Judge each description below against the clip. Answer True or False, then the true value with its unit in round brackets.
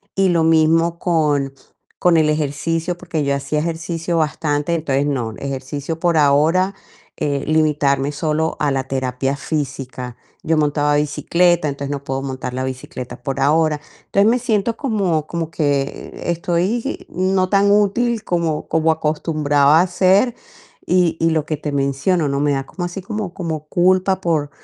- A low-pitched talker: False (155 Hz)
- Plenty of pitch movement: False (3.7 semitones)